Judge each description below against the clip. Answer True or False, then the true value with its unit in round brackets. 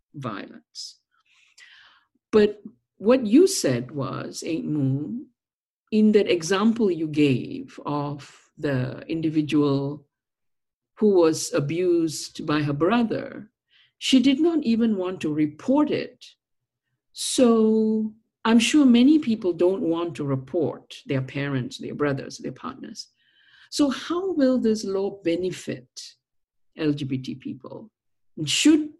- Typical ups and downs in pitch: False (8.3 semitones)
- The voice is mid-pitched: True (170 Hz)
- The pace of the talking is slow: True (115 wpm)